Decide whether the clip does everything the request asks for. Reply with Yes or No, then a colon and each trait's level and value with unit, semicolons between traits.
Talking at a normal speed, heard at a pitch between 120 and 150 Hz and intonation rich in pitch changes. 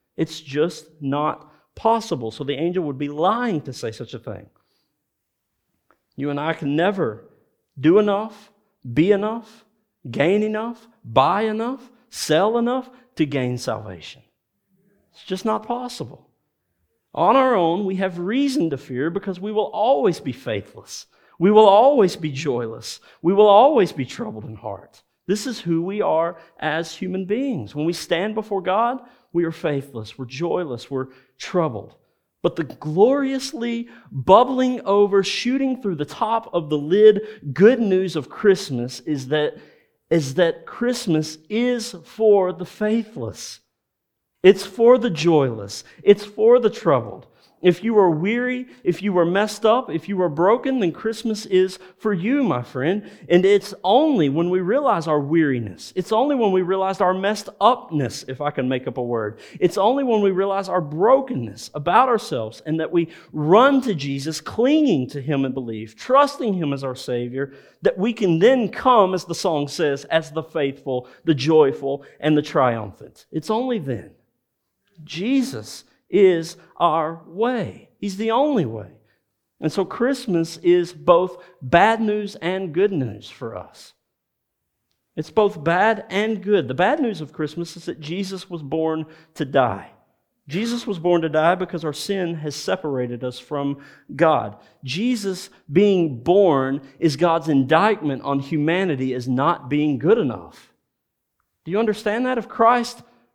No: average, 160 wpm; medium, 175 Hz; wide, 6.2 semitones